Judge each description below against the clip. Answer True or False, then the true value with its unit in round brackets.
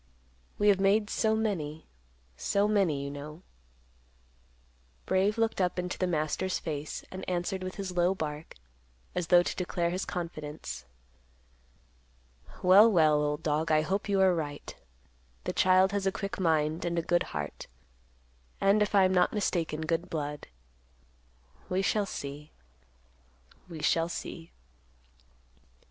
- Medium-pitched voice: True (175 Hz)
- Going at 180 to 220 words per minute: False (140 wpm)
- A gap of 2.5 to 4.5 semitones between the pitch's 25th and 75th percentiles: True (3.8 semitones)